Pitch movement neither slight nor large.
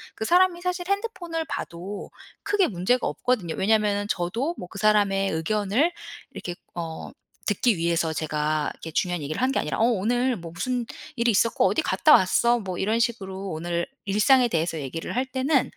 No: wide, 6.4 semitones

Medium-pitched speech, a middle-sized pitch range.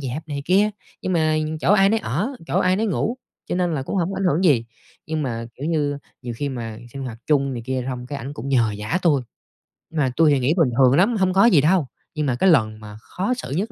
No: medium, 150 Hz; wide, 6.1 semitones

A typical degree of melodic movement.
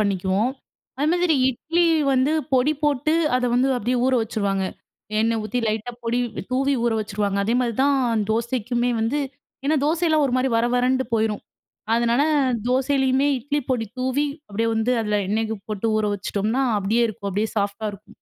Yes: average, 3.6 semitones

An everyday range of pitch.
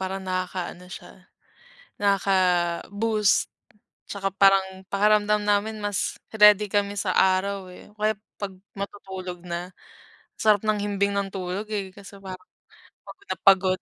No: narrow, 1.7 semitones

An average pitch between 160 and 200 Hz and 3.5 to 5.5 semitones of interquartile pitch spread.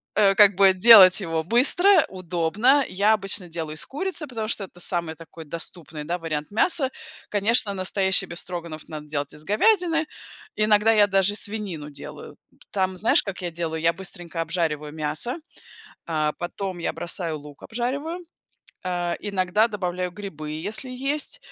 Yes: medium, 185 Hz; average, 4.7 semitones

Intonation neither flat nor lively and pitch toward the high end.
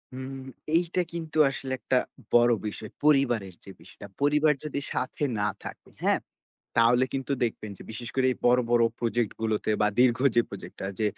No: average, 3.4 semitones; low, 125 Hz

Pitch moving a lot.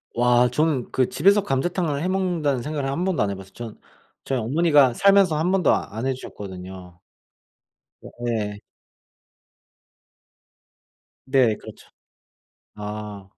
Yes: wide, 7.3 semitones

